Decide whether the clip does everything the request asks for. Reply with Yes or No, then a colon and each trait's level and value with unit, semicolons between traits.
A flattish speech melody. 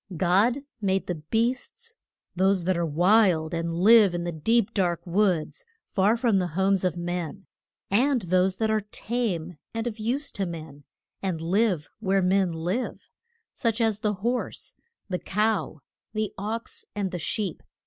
No: average, 4.2 semitones